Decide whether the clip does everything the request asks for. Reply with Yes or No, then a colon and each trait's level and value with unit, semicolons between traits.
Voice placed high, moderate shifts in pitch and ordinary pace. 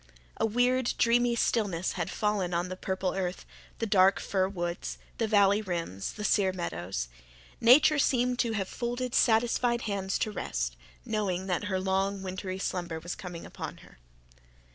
Yes: high, 195 Hz; average, 4.0 semitones; average, 160 wpm